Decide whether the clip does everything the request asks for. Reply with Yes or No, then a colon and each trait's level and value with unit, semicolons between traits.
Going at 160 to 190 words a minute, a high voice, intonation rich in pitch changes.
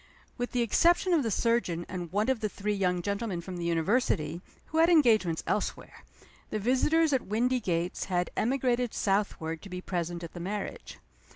Yes: average, 175 wpm; high, 205 Hz; wide, 5.7 semitones